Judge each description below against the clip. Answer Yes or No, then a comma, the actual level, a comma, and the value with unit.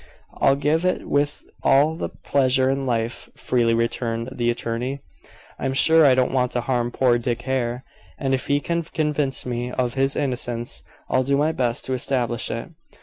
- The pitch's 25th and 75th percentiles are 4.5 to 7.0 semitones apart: No, narrow, 2.5 semitones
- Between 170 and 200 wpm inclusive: Yes, average, 180 wpm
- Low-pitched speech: Yes, low, 130 Hz